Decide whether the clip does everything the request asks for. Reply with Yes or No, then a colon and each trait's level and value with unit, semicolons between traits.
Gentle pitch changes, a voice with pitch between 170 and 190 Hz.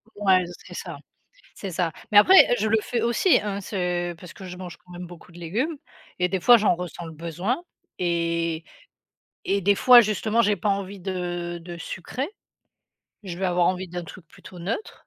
No: average, 3.0 semitones; medium, 185 Hz